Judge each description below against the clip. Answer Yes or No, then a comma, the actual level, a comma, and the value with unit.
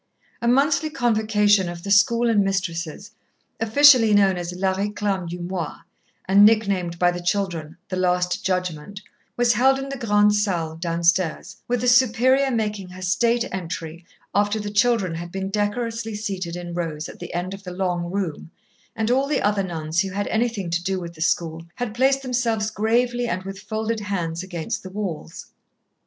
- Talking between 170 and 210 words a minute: Yes, average, 175 wpm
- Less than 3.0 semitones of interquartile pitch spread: No, average, 4.1 semitones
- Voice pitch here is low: No, high, 200 Hz